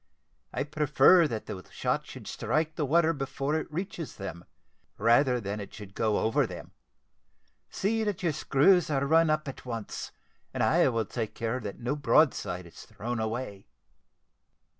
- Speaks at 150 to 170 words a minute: Yes, average, 160 wpm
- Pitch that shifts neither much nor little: No, wide, 5.8 semitones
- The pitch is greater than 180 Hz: No, low, 135 Hz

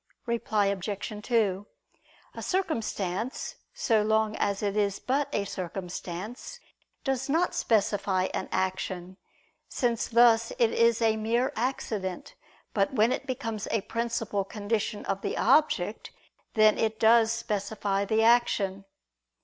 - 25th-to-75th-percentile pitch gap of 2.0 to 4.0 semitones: Yes, average, 2.9 semitones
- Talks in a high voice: Yes, high, 220 Hz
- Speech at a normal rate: No, slow, 125 wpm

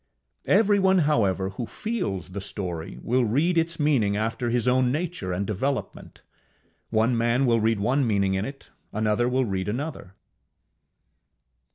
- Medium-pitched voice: No, low, 115 Hz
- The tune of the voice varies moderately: No, wide, 5.9 semitones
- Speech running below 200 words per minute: Yes, average, 145 wpm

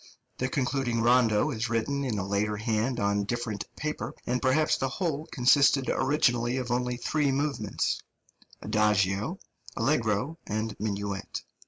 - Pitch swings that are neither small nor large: Yes, average, 4.0 semitones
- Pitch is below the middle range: Yes, low, 120 Hz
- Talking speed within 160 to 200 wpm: No, slow, 135 wpm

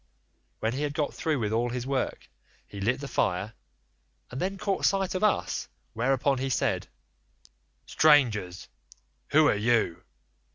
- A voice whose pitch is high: No, low, 130 Hz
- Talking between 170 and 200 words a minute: No, average, 150 wpm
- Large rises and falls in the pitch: No, average, 5.0 semitones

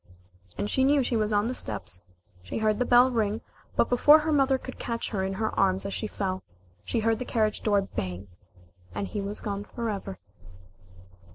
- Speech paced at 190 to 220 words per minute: Yes, average, 195 wpm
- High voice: Yes, high, 215 Hz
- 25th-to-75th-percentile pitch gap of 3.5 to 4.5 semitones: Yes, average, 3.8 semitones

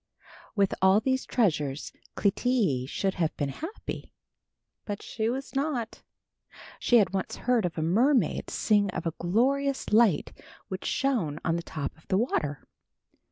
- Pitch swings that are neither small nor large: No, wide, 6.9 semitones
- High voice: Yes, high, 205 Hz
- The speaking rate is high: No, average, 145 wpm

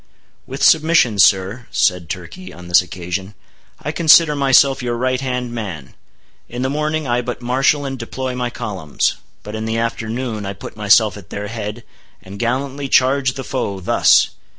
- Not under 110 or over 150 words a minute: No, average, 170 wpm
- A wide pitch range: No, average, 4.6 semitones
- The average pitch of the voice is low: Yes, low, 120 Hz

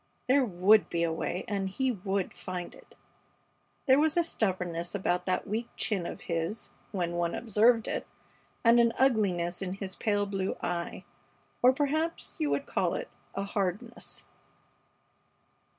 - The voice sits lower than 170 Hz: No, high, 200 Hz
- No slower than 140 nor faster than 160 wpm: Yes, average, 150 wpm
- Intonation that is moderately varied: Yes, average, 5.0 semitones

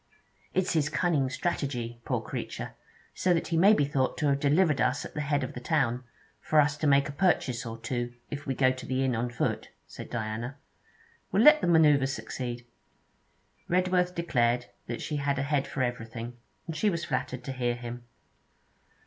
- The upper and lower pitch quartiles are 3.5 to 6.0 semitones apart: Yes, average, 4.1 semitones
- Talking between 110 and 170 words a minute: No, average, 195 wpm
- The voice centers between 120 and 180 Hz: Yes, medium, 140 Hz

